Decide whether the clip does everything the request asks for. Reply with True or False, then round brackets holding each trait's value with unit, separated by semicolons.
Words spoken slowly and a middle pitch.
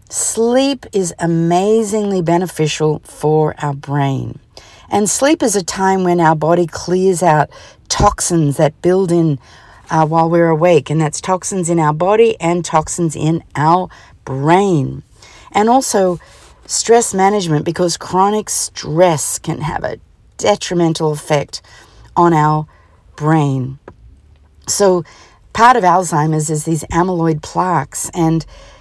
True (125 wpm; 165 Hz)